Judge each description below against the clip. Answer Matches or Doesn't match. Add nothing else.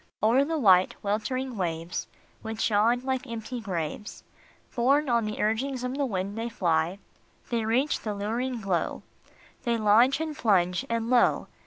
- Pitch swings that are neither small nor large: Matches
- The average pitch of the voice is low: Doesn't match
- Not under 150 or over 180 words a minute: Matches